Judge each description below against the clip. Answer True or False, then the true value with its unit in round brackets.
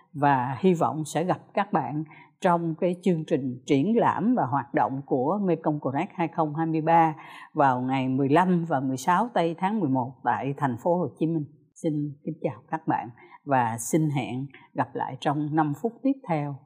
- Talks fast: False (175 wpm)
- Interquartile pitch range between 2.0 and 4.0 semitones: True (3.5 semitones)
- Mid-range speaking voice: True (155 Hz)